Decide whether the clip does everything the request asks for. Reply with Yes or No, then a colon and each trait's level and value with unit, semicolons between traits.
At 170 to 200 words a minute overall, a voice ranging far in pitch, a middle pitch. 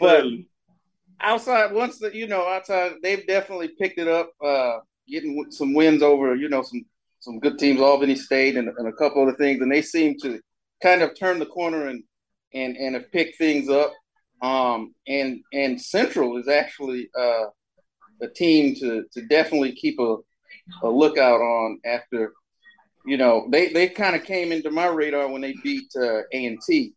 Yes: average, 175 wpm; wide, 5.7 semitones; medium, 150 Hz